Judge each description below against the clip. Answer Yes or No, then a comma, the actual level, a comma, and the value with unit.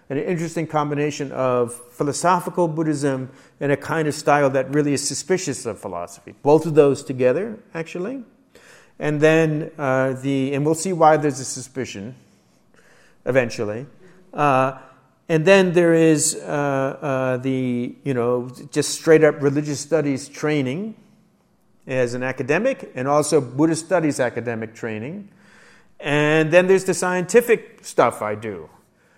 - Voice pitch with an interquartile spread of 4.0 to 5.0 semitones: Yes, average, 4.3 semitones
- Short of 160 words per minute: Yes, average, 140 wpm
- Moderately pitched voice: Yes, medium, 145 Hz